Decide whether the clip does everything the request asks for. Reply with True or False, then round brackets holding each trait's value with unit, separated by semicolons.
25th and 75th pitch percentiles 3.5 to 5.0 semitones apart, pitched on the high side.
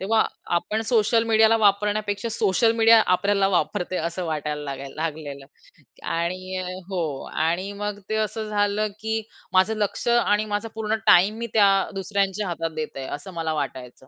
True (4.3 semitones; 200 Hz)